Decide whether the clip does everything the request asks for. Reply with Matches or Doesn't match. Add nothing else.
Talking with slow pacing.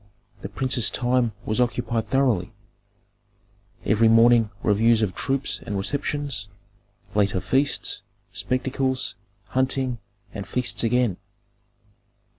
Matches